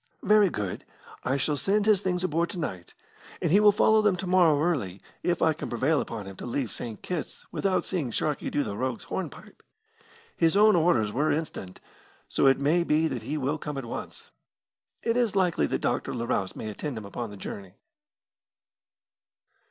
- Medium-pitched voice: Yes, medium, 150 Hz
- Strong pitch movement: Yes, wide, 7.3 semitones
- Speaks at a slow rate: No, average, 190 wpm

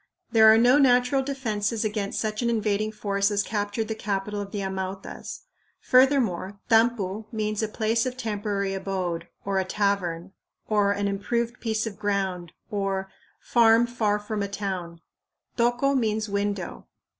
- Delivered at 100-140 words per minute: No, average, 150 wpm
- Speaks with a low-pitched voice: No, high, 210 Hz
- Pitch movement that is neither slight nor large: No, narrow, 2.3 semitones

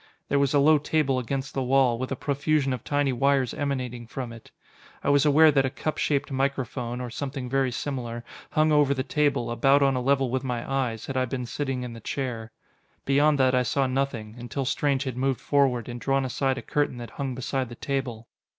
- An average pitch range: No, narrow, 2.1 semitones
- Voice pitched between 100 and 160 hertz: Yes, low, 135 Hz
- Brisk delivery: Yes, fast, 215 wpm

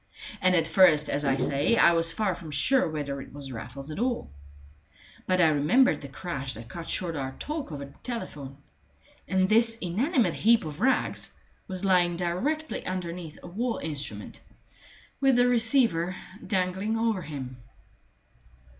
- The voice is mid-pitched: Yes, medium, 175 Hz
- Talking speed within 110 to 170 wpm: Yes, average, 155 wpm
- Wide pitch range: Yes, wide, 7.3 semitones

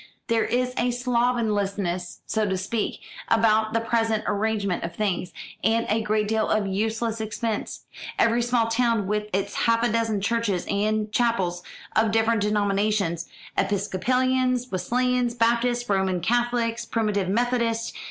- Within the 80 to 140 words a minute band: Yes, slow, 135 wpm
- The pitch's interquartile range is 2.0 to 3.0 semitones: Yes, narrow, 2.5 semitones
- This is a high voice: Yes, high, 220 Hz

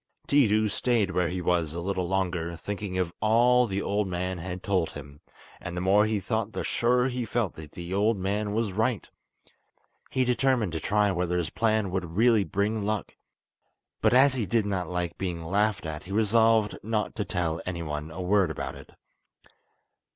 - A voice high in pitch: No, low, 100 Hz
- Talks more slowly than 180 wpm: No, average, 185 wpm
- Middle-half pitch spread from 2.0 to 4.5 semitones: Yes, average, 3.7 semitones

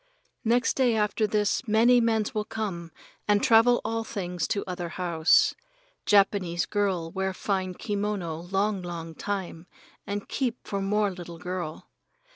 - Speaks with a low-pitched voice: No, high, 200 Hz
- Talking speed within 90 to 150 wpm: Yes, average, 140 wpm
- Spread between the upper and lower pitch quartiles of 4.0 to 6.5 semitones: No, average, 3.3 semitones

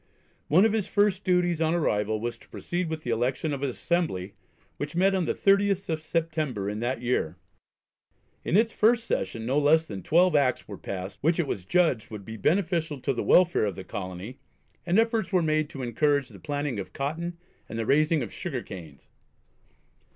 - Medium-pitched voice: Yes, medium, 150 Hz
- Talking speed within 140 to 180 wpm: No, average, 195 wpm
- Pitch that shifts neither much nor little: No, wide, 7.3 semitones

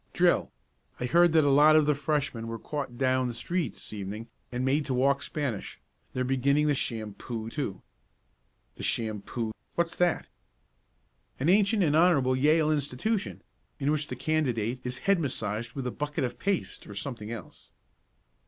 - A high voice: No, low, 135 Hz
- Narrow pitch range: No, average, 4.6 semitones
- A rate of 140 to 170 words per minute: Yes, average, 165 wpm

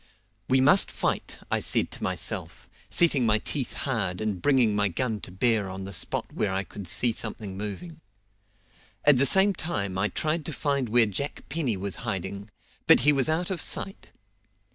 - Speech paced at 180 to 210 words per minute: Yes, average, 185 wpm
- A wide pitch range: Yes, wide, 6.6 semitones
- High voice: No, low, 115 Hz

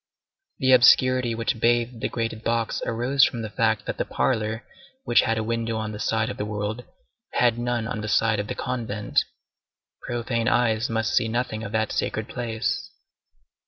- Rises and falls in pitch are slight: Yes, narrow, 1.5 semitones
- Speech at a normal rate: Yes, average, 180 wpm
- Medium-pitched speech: No, low, 115 Hz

